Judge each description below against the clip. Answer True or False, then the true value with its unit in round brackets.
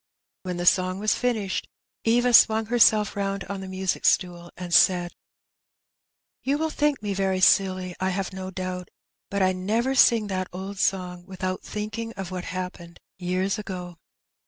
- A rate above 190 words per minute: False (165 wpm)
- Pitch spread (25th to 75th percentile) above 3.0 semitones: False (2.5 semitones)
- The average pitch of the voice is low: False (190 Hz)